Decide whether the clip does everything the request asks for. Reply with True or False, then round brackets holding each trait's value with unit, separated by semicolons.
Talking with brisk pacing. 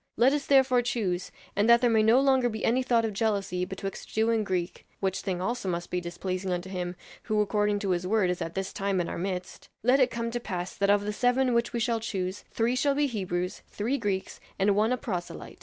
True (240 wpm)